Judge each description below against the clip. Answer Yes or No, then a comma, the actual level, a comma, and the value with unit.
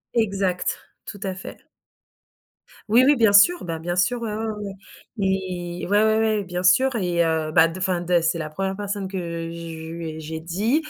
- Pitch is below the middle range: No, medium, 185 Hz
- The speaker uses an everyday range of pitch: Yes, average, 3.7 semitones